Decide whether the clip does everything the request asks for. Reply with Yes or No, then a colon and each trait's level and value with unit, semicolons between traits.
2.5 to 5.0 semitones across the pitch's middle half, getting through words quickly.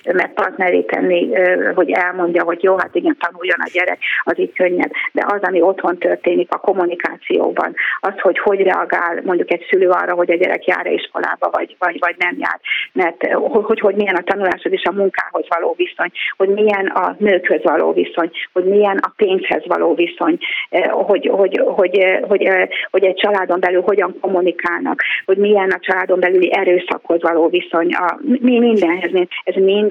Yes: average, 2.8 semitones; fast, 170 wpm